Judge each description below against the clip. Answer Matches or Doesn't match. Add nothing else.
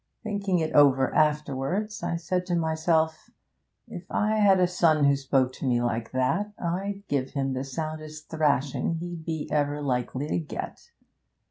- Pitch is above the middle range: Doesn't match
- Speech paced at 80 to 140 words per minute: Doesn't match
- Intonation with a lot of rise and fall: Doesn't match